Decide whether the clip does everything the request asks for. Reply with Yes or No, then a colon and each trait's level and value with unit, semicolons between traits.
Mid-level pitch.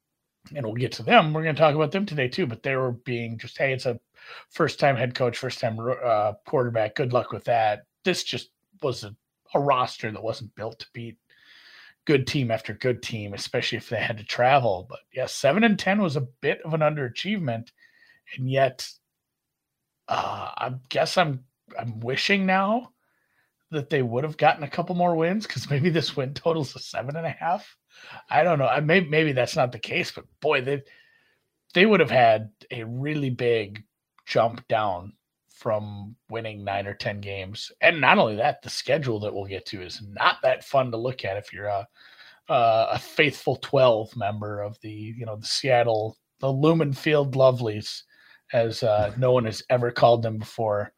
No: low, 125 Hz